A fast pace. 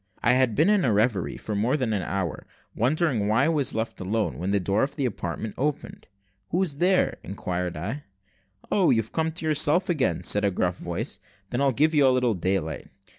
Yes: fast, 210 wpm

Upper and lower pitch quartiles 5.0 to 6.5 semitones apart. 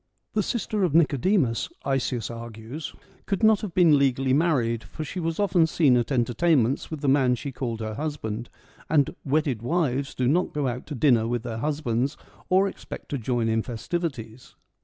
Yes: average, 5.3 semitones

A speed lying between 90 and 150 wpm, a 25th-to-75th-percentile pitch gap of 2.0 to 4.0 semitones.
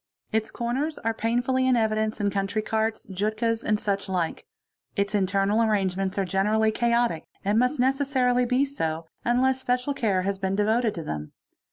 No: average, 165 wpm; average, 3.7 semitones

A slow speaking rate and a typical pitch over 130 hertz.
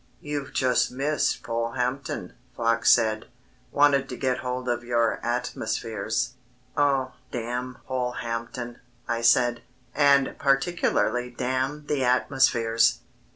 No: slow, 105 wpm; low, 125 Hz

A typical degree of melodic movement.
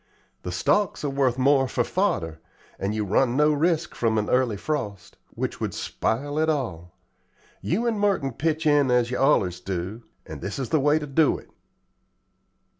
No: wide, 6.2 semitones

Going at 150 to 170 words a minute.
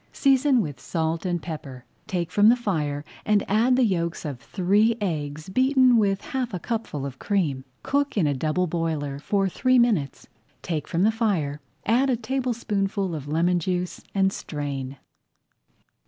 Yes: average, 160 wpm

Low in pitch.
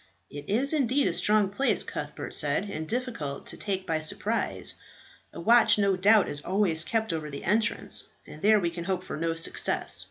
No: high, 195 Hz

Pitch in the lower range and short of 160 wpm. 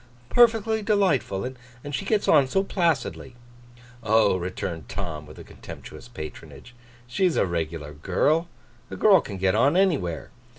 Yes: low, 120 Hz; slow, 135 wpm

